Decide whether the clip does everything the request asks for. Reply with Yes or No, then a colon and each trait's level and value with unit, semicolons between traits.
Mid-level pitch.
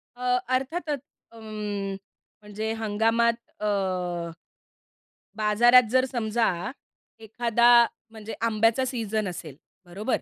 No: high, 225 Hz